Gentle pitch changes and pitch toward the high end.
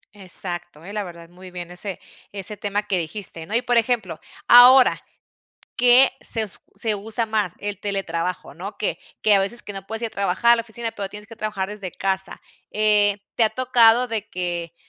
No: average, 3.4 semitones; high, 205 Hz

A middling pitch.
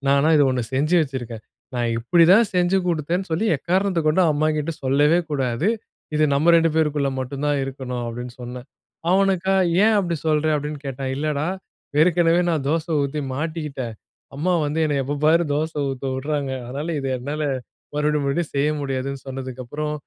Yes: medium, 150 Hz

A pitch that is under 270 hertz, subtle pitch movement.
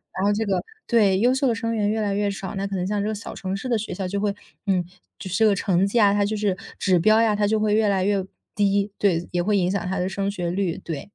Yes: high, 200 Hz; narrow, 1.8 semitones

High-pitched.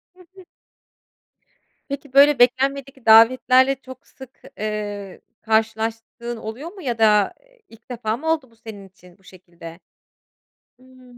Yes: high, 235 Hz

